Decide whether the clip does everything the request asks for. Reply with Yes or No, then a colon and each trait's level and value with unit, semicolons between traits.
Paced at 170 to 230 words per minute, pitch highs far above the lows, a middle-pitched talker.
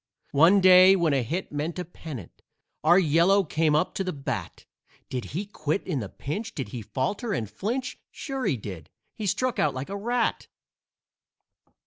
Yes: average, 175 wpm; wide, 5.9 semitones; medium, 170 Hz